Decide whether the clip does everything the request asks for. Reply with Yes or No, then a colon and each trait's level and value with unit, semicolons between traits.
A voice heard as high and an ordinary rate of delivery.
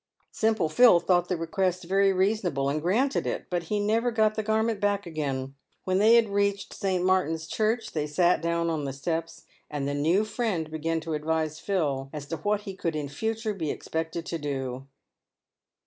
No: medium, 175 Hz; average, 190 wpm